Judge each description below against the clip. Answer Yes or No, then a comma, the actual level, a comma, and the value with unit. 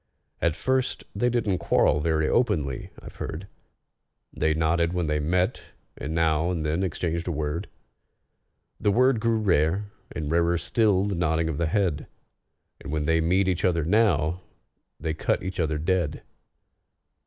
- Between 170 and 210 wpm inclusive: No, average, 155 wpm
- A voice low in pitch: Yes, very low, 85 Hz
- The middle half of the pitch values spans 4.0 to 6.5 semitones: No, average, 3.4 semitones